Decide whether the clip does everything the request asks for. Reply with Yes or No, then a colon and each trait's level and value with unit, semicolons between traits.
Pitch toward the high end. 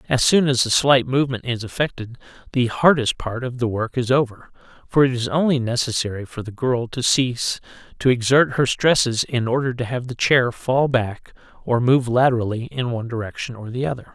No: low, 125 Hz